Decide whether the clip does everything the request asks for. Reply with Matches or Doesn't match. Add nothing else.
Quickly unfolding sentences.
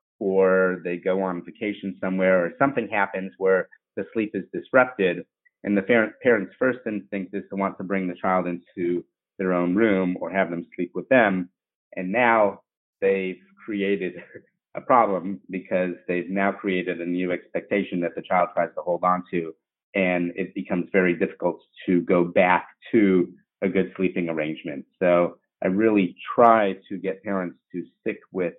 Doesn't match